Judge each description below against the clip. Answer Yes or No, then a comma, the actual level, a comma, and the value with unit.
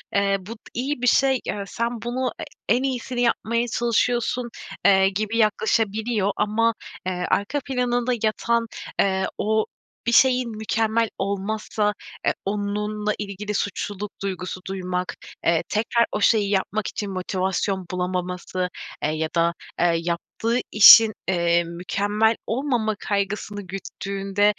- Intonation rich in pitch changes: No, average, 3.2 semitones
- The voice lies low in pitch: No, high, 210 Hz